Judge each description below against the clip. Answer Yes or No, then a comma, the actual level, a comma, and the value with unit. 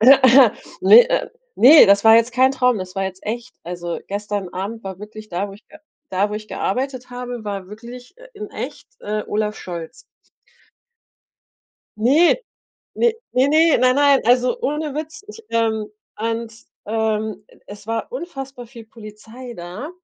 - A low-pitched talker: No, high, 230 Hz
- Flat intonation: No, average, 4.1 semitones